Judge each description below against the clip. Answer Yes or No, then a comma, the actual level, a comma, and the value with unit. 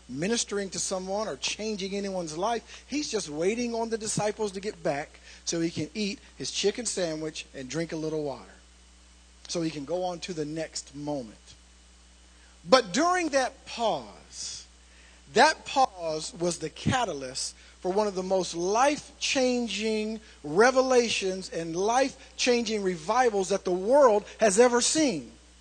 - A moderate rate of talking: Yes, average, 150 wpm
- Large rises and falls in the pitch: Yes, wide, 7.1 semitones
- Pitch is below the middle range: No, medium, 185 Hz